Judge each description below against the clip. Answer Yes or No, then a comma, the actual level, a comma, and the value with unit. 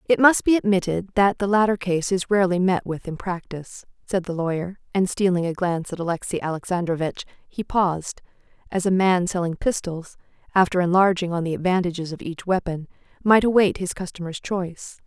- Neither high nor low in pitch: Yes, medium, 180 Hz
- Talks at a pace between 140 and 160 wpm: No, average, 175 wpm